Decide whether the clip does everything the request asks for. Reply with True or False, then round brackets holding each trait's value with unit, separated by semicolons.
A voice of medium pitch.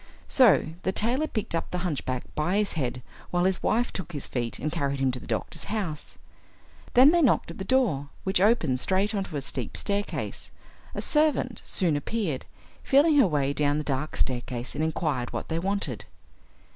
True (170 Hz)